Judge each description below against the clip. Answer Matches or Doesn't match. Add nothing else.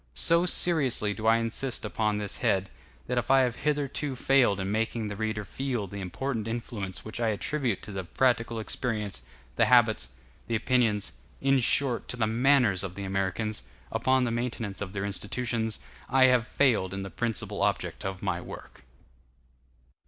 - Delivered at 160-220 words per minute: Matches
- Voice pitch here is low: Matches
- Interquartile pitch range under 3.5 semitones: Doesn't match